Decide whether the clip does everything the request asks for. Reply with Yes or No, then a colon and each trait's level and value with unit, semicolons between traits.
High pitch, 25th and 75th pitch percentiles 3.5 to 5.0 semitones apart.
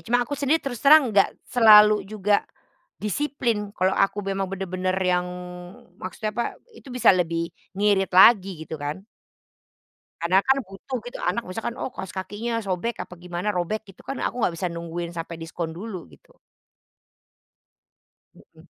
Yes: high, 195 Hz; average, 4.4 semitones